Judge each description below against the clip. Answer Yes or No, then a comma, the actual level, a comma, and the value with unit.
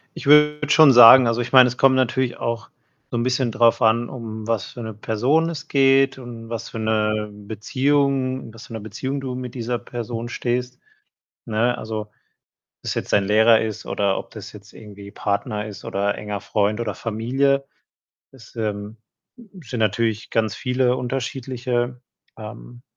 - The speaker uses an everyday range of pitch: Yes, average, 3.1 semitones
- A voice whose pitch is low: Yes, low, 115 Hz